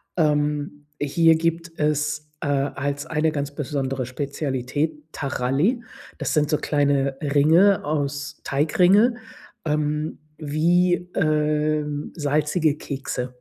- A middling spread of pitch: No, narrow, 1.8 semitones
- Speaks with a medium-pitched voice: Yes, medium, 150 Hz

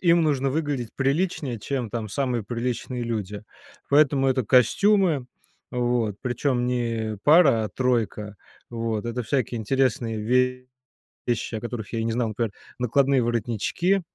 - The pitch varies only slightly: No, average, 3.3 semitones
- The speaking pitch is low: Yes, low, 120 Hz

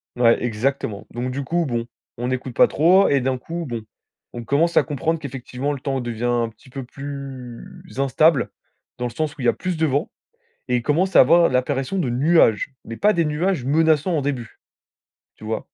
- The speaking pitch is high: No, low, 135 Hz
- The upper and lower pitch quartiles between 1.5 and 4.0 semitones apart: No, average, 4.5 semitones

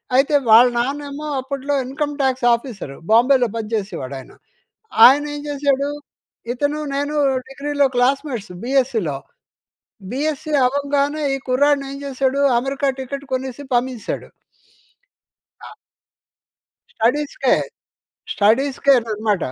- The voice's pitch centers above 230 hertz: Yes, very high, 270 Hz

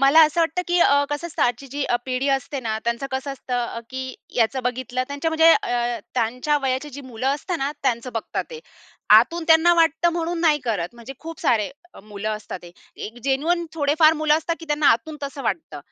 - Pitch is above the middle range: Yes, very high, 275 Hz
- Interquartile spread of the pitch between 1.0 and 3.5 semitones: No, average, 4.8 semitones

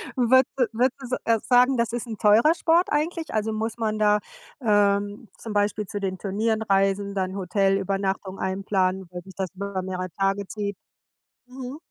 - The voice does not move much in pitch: No, average, 3.3 semitones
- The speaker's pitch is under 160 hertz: No, high, 205 Hz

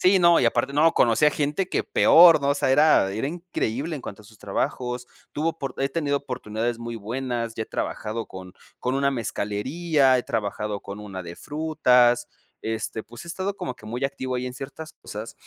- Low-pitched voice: Yes, low, 125 Hz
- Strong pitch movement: No, average, 4.8 semitones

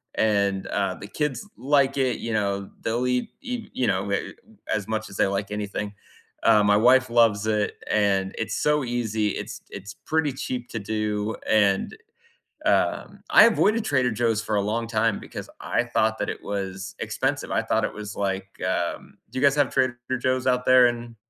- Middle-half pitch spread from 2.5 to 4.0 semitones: Yes, average, 3.7 semitones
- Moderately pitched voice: No, low, 110 Hz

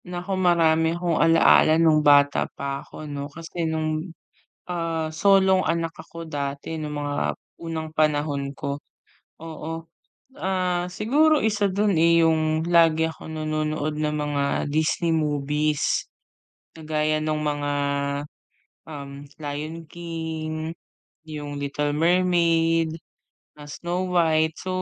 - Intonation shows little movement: Yes, narrow, 1.9 semitones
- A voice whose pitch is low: No, medium, 160 Hz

